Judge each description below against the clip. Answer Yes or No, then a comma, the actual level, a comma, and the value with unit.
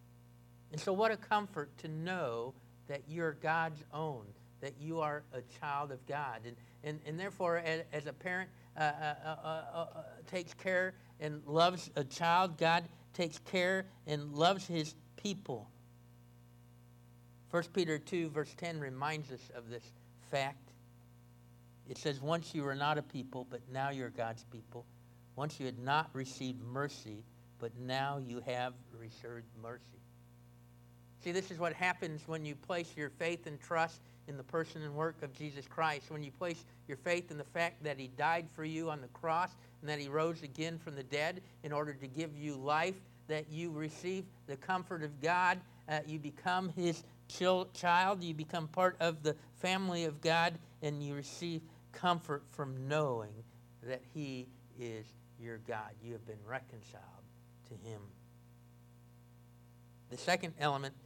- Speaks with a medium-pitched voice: Yes, medium, 145 Hz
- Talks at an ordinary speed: Yes, average, 165 wpm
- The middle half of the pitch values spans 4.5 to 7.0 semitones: Yes, average, 5.3 semitones